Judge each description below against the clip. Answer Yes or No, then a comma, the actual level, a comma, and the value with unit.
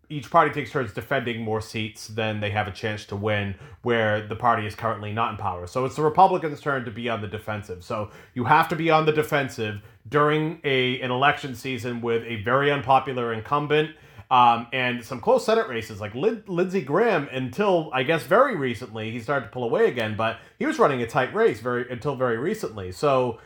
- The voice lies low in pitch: Yes, low, 125 Hz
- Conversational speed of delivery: No, fast, 210 wpm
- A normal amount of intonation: Yes, average, 4.6 semitones